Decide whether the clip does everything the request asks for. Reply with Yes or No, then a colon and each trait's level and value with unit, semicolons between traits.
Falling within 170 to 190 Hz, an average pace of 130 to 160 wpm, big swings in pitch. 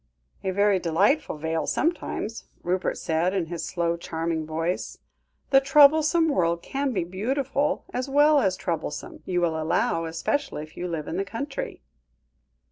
Yes: medium, 185 Hz; average, 150 wpm; wide, 8.5 semitones